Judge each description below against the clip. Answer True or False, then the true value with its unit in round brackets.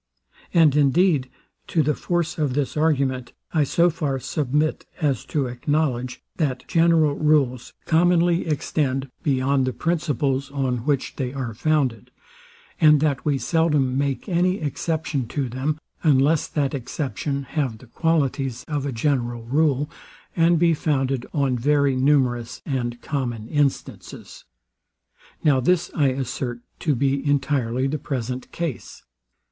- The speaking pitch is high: False (140 Hz)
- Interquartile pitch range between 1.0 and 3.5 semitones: True (3.1 semitones)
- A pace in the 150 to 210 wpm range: False (135 wpm)